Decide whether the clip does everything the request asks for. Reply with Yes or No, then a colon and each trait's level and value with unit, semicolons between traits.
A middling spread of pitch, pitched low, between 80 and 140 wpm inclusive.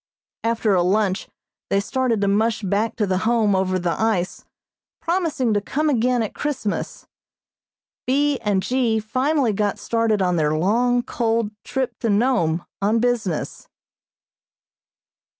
No: average, 3.7 semitones; high, 220 Hz; slow, 135 wpm